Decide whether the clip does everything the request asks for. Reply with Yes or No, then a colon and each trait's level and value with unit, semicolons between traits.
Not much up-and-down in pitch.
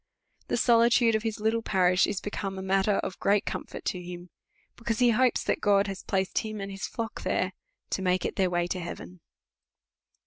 No: average, 3.2 semitones